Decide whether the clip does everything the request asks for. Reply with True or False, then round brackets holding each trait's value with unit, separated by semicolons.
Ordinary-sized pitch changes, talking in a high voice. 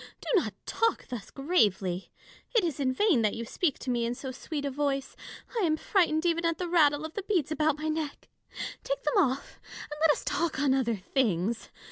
True (4.8 semitones; 290 Hz)